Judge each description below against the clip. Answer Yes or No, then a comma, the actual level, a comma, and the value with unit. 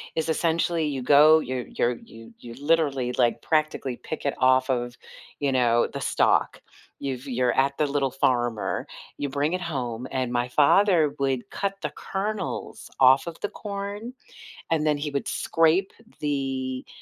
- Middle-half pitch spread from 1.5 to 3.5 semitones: No, average, 3.9 semitones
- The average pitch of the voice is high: No, medium, 140 Hz